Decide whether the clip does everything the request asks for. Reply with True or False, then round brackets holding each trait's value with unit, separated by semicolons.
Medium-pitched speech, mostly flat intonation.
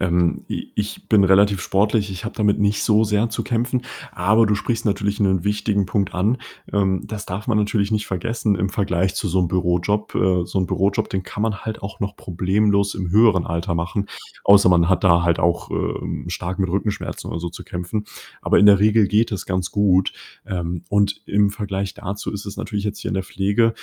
False (100 Hz; 2.1 semitones)